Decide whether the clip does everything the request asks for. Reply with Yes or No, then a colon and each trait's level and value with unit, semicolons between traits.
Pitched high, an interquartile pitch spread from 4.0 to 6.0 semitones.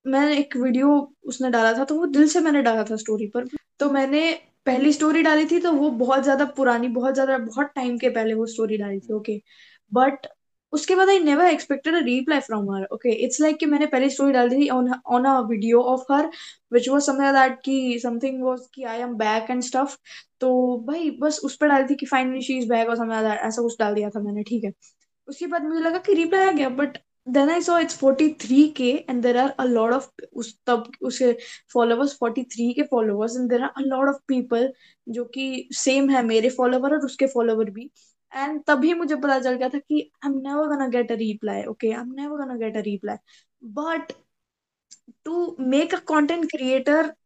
No: very high, 265 Hz; average, 3.4 semitones